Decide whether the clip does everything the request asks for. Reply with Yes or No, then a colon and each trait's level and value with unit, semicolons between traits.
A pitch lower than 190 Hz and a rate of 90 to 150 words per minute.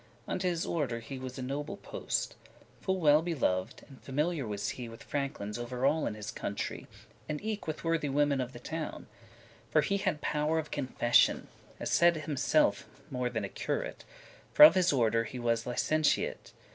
No: medium, 140 Hz; average, 185 wpm